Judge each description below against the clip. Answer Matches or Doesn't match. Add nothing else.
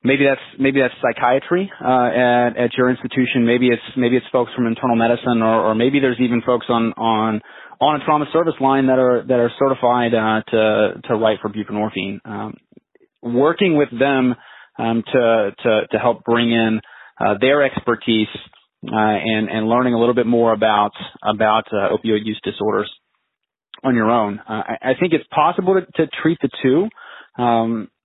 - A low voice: Matches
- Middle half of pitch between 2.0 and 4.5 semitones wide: Matches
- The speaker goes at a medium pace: Matches